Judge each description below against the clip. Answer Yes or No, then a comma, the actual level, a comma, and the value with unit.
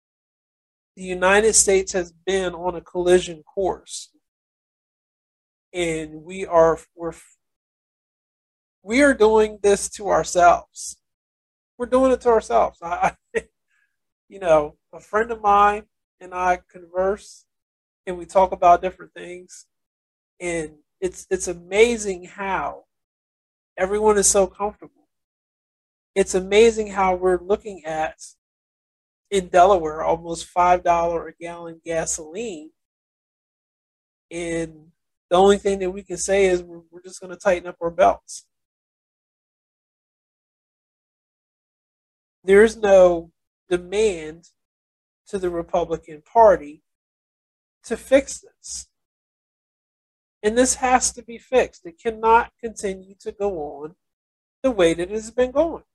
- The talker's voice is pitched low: No, medium, 185 Hz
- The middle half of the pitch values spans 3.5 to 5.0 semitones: Yes, average, 3.8 semitones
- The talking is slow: Yes, slow, 120 wpm